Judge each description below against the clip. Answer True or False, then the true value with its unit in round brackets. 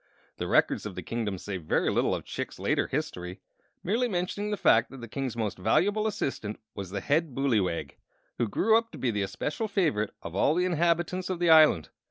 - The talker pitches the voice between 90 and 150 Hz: True (140 Hz)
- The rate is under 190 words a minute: False (205 wpm)